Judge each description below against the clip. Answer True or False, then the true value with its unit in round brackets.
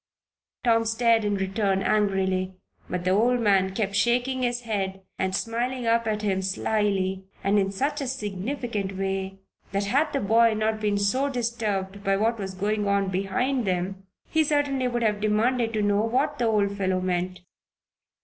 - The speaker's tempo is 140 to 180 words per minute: True (170 wpm)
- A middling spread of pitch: True (3.4 semitones)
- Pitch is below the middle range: False (210 Hz)